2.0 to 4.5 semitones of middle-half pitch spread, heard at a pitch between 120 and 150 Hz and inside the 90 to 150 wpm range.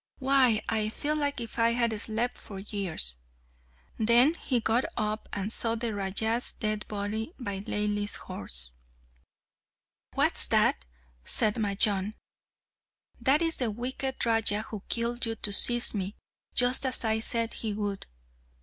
No: average, 2.8 semitones; high, 220 Hz; average, 140 wpm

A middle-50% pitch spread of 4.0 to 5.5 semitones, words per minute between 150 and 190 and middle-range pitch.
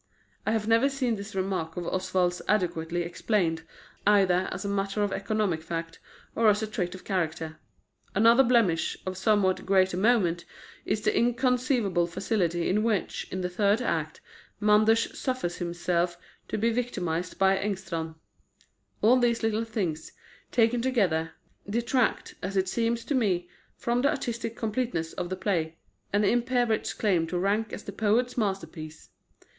No: average, 4.5 semitones; average, 155 wpm; high, 200 Hz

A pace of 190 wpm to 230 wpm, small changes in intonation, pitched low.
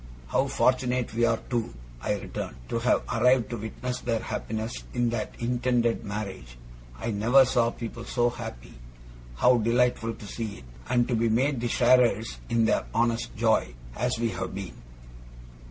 No: average, 165 wpm; narrow, 1.8 semitones; low, 115 Hz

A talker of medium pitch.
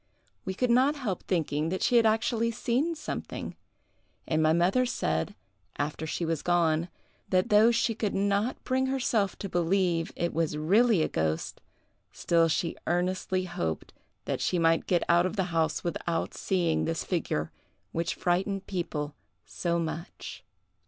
Yes: medium, 175 Hz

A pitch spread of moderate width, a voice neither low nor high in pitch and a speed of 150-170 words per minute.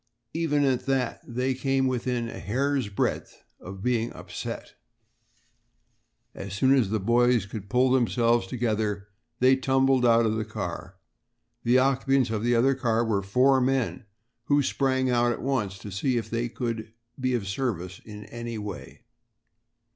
No: average, 3.3 semitones; low, 120 Hz; average, 160 wpm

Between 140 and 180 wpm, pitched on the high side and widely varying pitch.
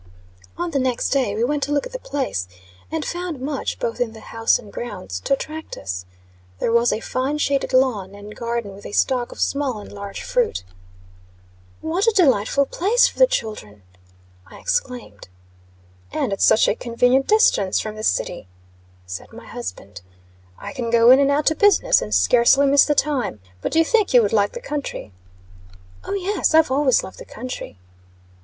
No: average, 190 wpm; very high, 255 Hz; wide, 6.0 semitones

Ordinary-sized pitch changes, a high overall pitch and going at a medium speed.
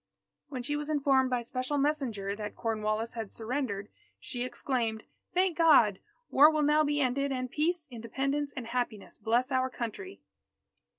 Yes: average, 4.3 semitones; very high, 255 Hz; average, 155 wpm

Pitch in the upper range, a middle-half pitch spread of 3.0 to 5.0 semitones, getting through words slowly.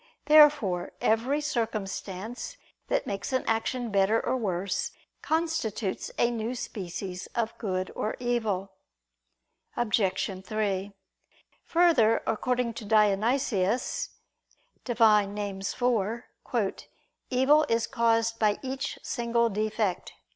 Yes: high, 225 Hz; average, 3.5 semitones; slow, 100 wpm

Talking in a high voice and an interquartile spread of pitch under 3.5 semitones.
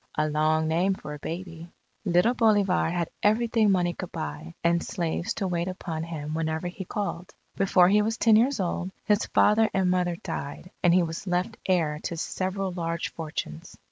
No: medium, 175 Hz; average, 3.1 semitones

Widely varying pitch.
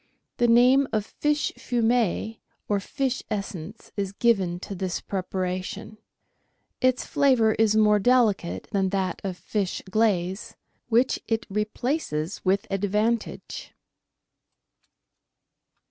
No: average, 3.6 semitones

